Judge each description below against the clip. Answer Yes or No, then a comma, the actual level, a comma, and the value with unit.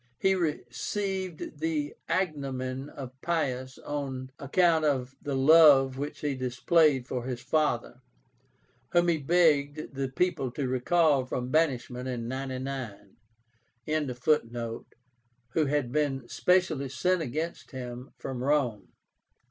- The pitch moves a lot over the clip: No, average, 3.5 semitones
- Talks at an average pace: No, slow, 115 wpm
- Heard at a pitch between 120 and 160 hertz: Yes, medium, 140 Hz